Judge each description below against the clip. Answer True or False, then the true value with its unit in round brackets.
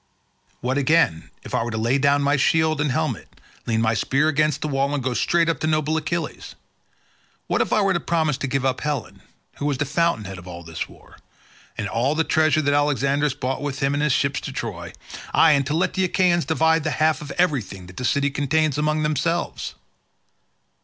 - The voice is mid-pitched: True (145 Hz)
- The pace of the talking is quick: True (215 wpm)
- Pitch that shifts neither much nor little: True (3.0 semitones)